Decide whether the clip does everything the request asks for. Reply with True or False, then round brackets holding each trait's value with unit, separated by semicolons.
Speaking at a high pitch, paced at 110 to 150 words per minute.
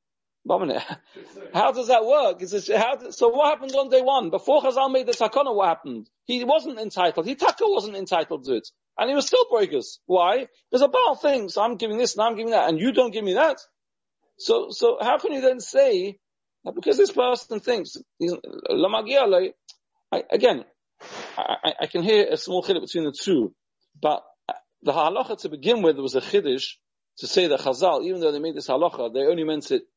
False (260 Hz; 200 wpm)